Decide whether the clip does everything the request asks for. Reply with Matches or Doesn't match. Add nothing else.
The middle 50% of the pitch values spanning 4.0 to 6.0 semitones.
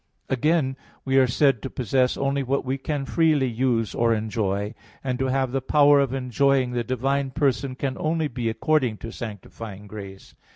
Doesn't match